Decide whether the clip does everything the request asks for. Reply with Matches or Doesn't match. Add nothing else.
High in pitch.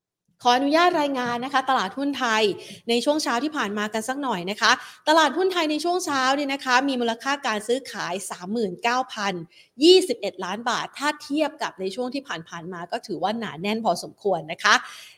Matches